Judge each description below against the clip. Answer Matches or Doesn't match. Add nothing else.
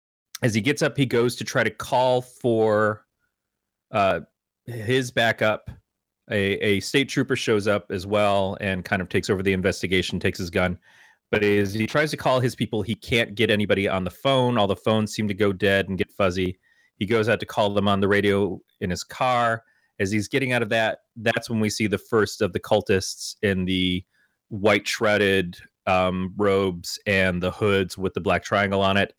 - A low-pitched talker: Matches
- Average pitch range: Matches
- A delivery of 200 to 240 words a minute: Matches